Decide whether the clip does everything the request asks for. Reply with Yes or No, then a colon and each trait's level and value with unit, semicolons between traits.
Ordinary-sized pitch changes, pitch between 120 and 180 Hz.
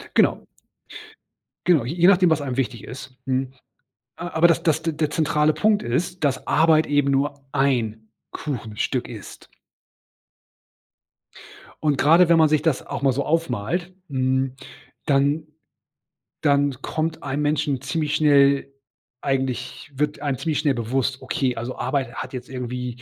Yes: average, 3.1 semitones; medium, 140 Hz